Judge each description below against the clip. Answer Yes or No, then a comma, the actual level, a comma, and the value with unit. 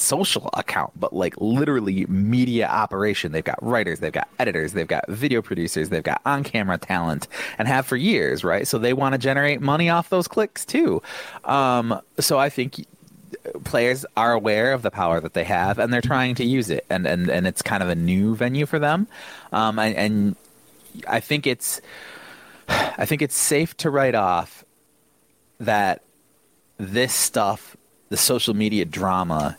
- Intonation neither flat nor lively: No, wide, 5.7 semitones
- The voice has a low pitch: Yes, low, 125 Hz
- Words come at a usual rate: Yes, average, 175 wpm